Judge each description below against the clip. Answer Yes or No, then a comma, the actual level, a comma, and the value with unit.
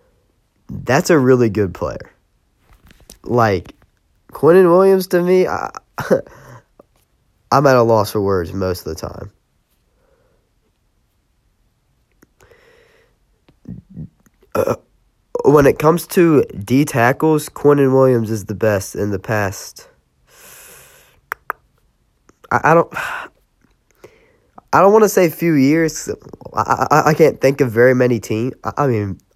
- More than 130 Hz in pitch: Yes, medium, 140 Hz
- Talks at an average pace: No, slow, 120 wpm